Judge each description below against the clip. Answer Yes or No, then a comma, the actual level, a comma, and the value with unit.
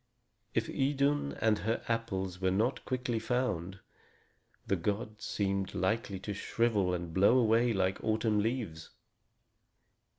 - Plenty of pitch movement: No, average, 3.7 semitones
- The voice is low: Yes, low, 110 Hz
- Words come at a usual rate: No, slow, 125 wpm